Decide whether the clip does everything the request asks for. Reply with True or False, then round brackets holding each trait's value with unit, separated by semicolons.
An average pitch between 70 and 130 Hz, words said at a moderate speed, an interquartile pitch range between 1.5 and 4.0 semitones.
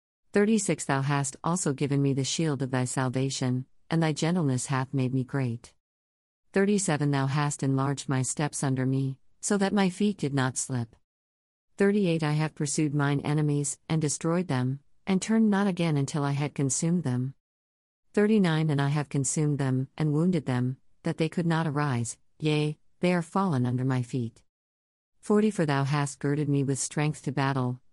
False (140 Hz; 175 wpm; 3.7 semitones)